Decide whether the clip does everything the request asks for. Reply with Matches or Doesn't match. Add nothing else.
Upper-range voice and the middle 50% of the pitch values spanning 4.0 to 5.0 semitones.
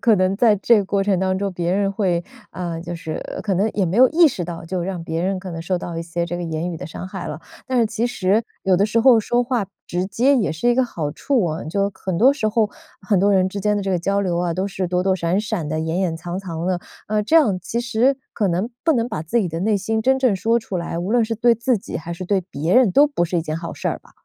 Matches